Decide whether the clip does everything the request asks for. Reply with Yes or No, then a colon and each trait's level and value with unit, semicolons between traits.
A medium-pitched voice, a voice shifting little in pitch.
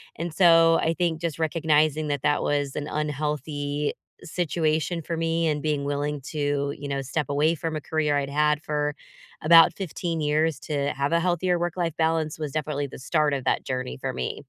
Yes: medium, 150 Hz; narrow, 2.2 semitones